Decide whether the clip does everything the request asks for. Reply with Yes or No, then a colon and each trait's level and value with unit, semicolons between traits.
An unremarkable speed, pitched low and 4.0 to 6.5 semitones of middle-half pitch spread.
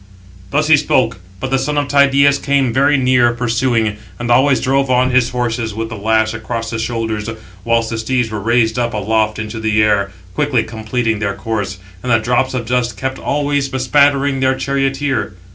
No: average, 185 wpm; low, 120 Hz; average, 3.2 semitones